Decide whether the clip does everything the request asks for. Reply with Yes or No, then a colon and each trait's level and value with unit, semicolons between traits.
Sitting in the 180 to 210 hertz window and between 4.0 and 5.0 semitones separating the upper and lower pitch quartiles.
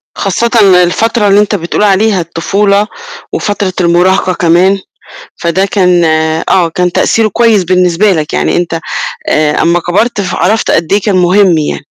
No: medium, 185 Hz; average, 2.9 semitones